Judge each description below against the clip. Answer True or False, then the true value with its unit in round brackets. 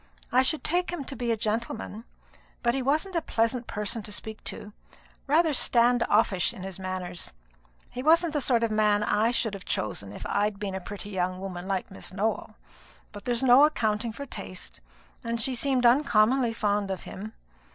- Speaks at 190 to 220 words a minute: True (195 wpm)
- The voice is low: False (225 Hz)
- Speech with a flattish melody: False (3.8 semitones)